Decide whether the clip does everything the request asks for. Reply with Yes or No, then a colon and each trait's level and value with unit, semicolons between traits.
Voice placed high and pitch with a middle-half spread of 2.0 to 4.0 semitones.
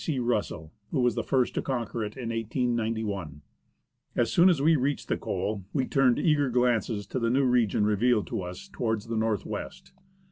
No: low, 120 Hz; average, 3.3 semitones